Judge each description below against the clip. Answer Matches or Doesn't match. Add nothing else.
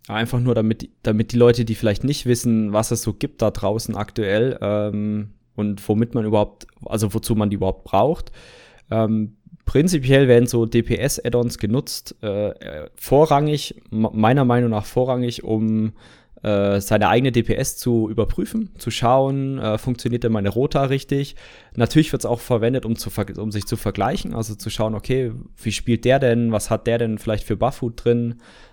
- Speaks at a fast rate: Doesn't match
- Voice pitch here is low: Matches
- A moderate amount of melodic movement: Doesn't match